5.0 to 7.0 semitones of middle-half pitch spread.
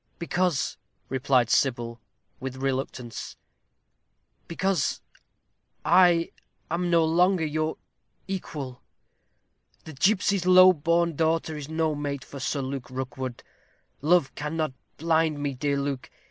No: average, 4.1 semitones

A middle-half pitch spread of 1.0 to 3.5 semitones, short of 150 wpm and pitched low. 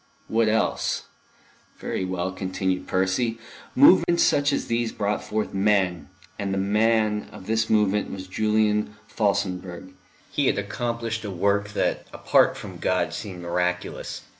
Yes: average, 2.8 semitones; average, 140 wpm; low, 105 Hz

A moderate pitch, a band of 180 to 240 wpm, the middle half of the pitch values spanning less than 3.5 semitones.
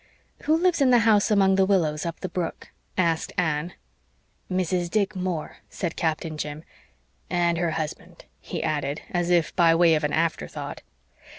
No: medium, 175 Hz; average, 165 wpm; average, 3.0 semitones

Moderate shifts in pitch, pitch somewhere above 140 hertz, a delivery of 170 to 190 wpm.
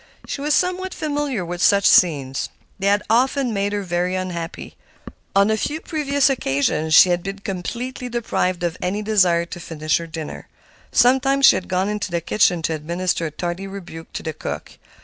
No: wide, 5.7 semitones; high, 190 Hz; average, 185 wpm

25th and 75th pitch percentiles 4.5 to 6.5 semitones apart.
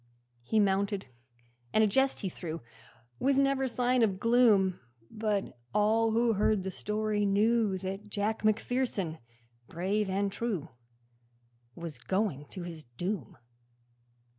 No: average, 3.0 semitones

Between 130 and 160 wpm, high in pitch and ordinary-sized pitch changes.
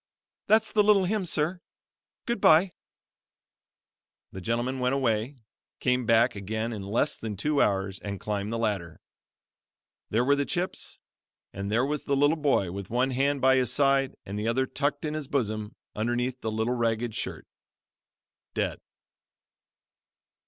No: average, 150 wpm; low, 125 Hz; average, 4.7 semitones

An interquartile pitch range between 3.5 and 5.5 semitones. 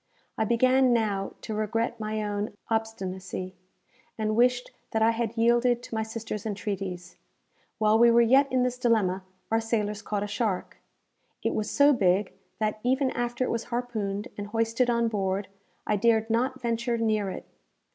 No: narrow, 2.4 semitones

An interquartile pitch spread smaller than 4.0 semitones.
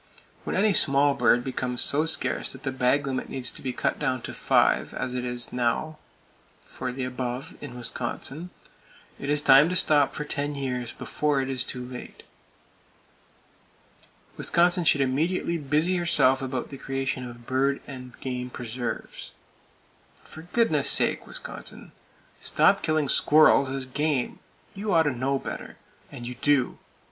Yes: average, 2.9 semitones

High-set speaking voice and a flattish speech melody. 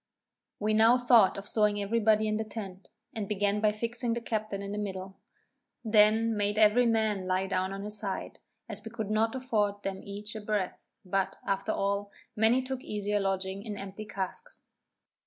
Yes: high, 210 Hz; narrow, 2.0 semitones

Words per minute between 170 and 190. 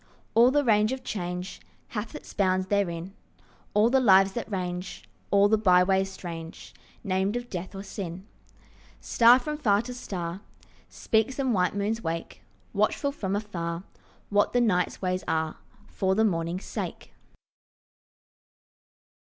No: average, 140 wpm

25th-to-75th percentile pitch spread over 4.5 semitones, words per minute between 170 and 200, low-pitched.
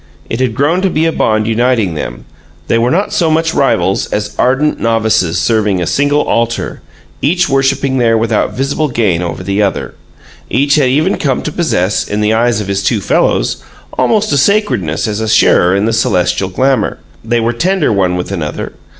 Yes: wide, 5.5 semitones; average, 190 wpm; low, 115 Hz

